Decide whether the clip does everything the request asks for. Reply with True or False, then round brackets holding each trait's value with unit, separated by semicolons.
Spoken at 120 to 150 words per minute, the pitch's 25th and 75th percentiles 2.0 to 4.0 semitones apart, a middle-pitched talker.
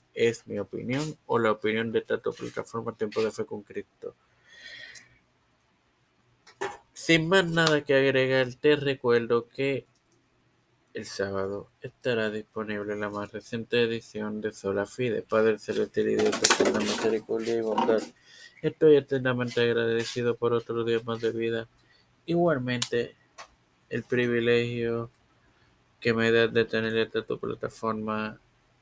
False (130 wpm; 3.0 semitones; 115 Hz)